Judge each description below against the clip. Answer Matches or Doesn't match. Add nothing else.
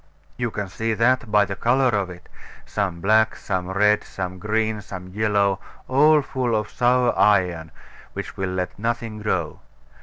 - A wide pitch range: Doesn't match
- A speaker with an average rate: Matches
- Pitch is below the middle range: Matches